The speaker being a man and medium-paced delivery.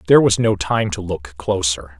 No: male; fast, 210 wpm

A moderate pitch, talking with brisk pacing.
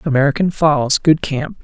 No: medium, 150 Hz; slow, 110 wpm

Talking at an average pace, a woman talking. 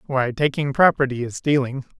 No: average, 150 wpm; male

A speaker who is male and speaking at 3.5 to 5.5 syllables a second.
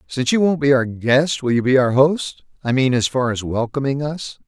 Yes: male; 5.1 syllables/s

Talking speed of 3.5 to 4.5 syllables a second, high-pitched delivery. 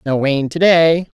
No: 4.0 syllables/s; medium, 155 Hz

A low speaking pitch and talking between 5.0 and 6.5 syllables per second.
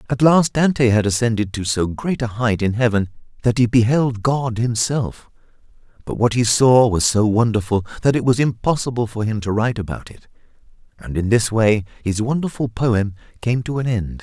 Yes: low, 115 Hz; 5.2 syllables/s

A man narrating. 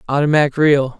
Yes: male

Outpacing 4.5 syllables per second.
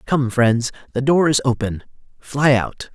No: 4.0 syllables/s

